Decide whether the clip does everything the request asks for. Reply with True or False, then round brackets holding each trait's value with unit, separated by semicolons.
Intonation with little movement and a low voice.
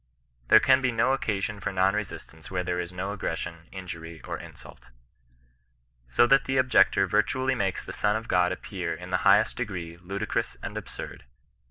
False (4.0 semitones; 95 Hz)